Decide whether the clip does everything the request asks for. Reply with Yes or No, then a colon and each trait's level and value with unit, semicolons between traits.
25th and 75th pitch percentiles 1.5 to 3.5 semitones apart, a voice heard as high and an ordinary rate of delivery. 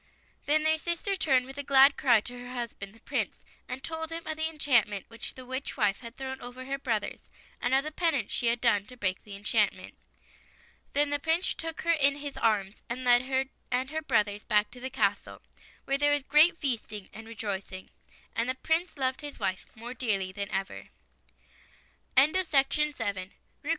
No: average, 4.7 semitones; very high, 255 Hz; average, 190 wpm